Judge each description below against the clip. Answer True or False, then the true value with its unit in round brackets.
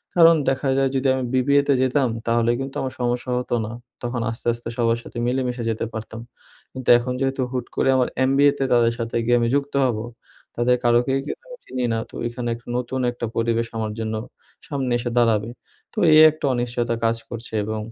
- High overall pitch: False (120 Hz)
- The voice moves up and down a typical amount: False (2.3 semitones)